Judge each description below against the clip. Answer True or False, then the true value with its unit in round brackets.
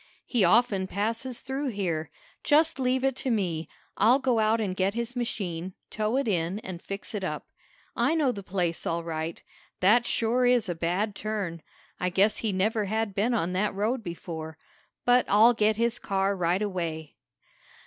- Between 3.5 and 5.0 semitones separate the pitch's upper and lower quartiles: True (4.5 semitones)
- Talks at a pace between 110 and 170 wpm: False (180 wpm)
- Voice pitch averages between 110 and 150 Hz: False (205 Hz)